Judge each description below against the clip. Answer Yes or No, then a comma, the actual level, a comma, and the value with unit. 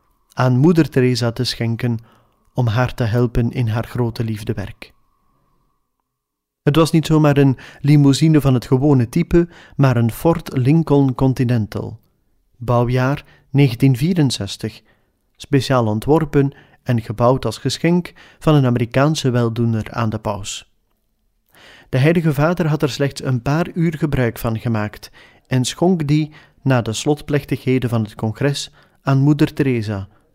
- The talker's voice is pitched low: Yes, low, 130 Hz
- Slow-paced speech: Yes, slow, 130 wpm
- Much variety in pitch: No, average, 4.1 semitones